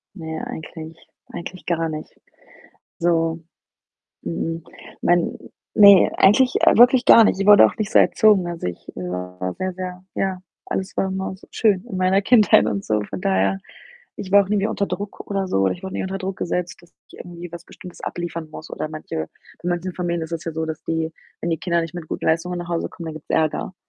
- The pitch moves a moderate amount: Yes, average, 3.0 semitones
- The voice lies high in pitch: No, medium, 175 Hz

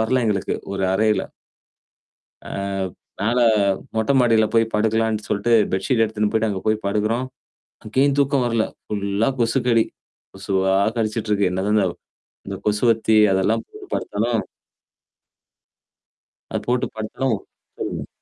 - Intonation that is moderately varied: No, narrow, 2.1 semitones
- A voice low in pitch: Yes, low, 110 Hz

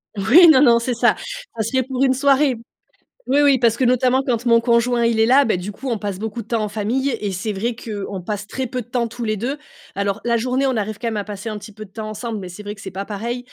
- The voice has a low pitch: No, high, 230 Hz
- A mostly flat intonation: No, average, 3.2 semitones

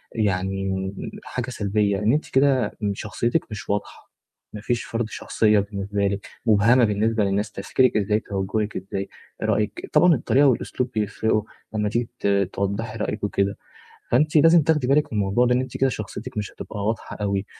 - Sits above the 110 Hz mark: No, low, 105 Hz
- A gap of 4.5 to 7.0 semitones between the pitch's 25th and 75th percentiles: No, average, 3.4 semitones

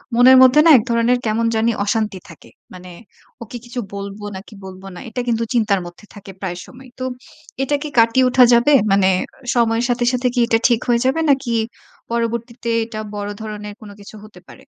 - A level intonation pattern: No, average, 3.2 semitones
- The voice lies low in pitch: No, high, 230 Hz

